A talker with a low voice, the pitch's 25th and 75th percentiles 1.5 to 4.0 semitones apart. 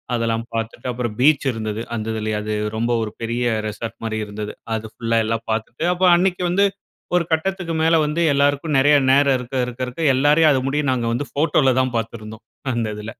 No: low, 125 Hz; average, 4.7 semitones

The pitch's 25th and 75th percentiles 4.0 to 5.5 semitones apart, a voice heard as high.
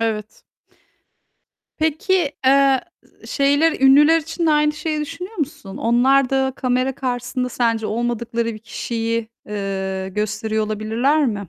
Yes: average, 4.8 semitones; very high, 250 Hz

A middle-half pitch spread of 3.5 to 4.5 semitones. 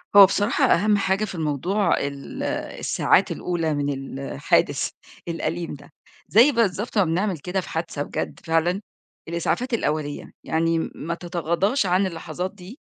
Yes: average, 3.8 semitones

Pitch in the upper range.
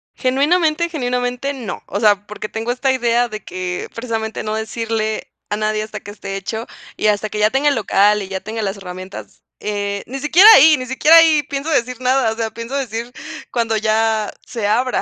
Yes: high, 225 Hz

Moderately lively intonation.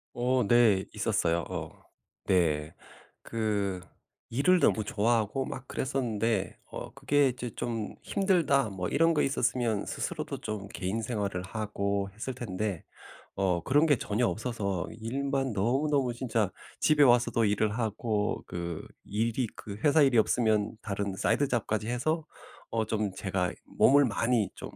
Yes: average, 4.1 semitones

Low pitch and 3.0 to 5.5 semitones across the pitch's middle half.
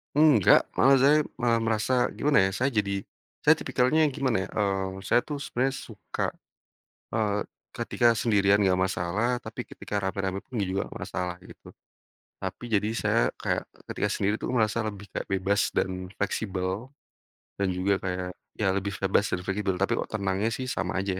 Yes: low, 100 Hz; average, 3.3 semitones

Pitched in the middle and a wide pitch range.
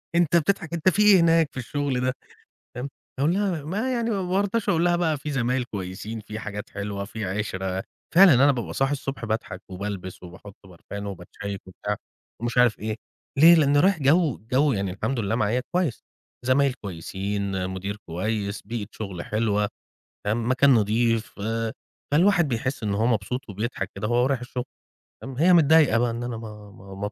No: low, 120 Hz; wide, 6.1 semitones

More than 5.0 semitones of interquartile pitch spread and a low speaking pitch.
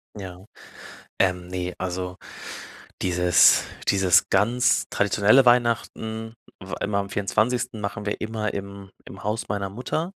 No: average, 2.9 semitones; low, 100 Hz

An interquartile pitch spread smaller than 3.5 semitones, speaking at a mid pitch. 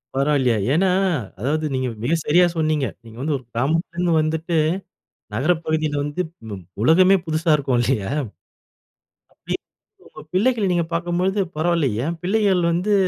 No: average, 3.8 semitones; medium, 160 Hz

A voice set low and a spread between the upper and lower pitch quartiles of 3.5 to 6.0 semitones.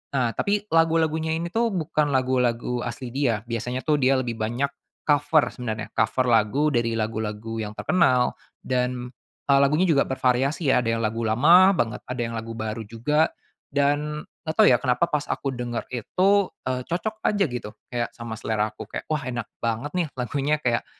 Yes: low, 125 Hz; average, 4.5 semitones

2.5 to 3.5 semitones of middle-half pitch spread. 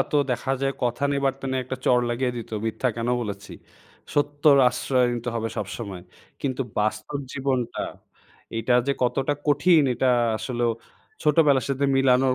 Yes: average, 2.8 semitones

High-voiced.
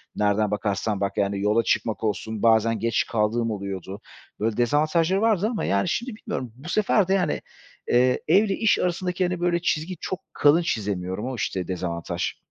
No: low, 115 Hz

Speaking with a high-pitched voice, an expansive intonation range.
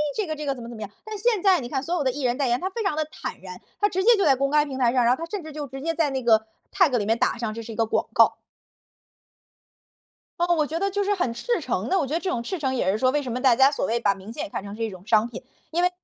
Yes: very high, 270 Hz; wide, 6.6 semitones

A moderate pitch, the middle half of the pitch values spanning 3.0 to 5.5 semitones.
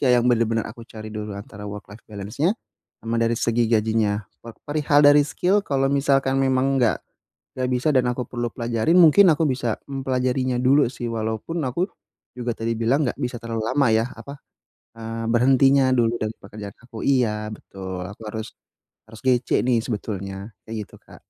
No: low, 120 Hz; average, 3.4 semitones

